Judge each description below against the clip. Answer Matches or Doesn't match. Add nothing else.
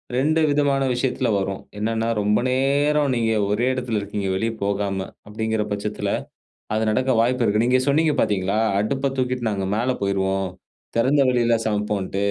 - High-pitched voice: Doesn't match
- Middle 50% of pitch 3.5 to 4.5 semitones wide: Matches